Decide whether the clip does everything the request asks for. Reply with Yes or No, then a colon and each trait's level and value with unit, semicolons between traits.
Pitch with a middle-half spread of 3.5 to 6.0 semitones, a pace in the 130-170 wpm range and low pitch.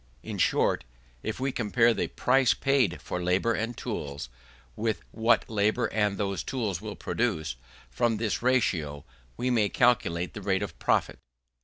Yes: average, 4.1 semitones; average, 160 wpm; low, 110 Hz